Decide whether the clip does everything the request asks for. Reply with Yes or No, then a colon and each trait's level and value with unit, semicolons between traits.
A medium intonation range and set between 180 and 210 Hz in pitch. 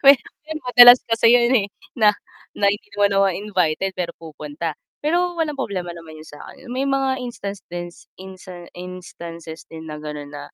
No: wide, 6.6 semitones; high, 190 Hz